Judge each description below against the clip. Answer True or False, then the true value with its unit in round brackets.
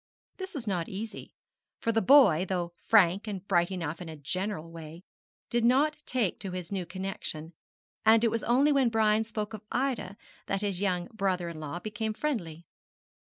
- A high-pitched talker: True (200 Hz)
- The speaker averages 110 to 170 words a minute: False (180 wpm)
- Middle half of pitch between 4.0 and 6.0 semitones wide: True (4.6 semitones)